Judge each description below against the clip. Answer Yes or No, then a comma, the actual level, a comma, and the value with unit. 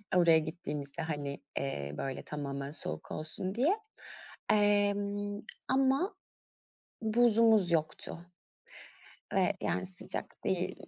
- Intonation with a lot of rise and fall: Yes, wide, 6.6 semitones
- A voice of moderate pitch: Yes, medium, 175 Hz